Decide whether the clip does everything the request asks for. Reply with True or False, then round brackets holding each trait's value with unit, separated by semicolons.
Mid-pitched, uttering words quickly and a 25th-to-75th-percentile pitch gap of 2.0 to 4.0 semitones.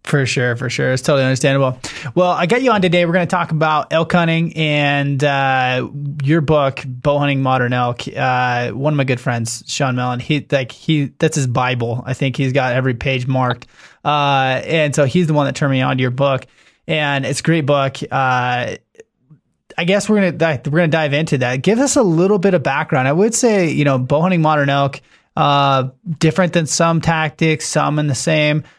True (145 Hz; 215 wpm; 3.7 semitones)